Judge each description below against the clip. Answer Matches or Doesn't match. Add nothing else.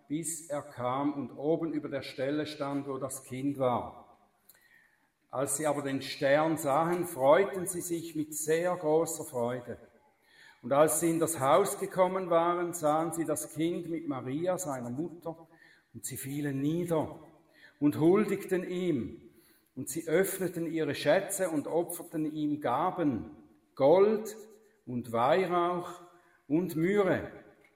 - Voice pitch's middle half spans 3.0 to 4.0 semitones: Matches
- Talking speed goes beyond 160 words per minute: Doesn't match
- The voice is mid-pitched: Matches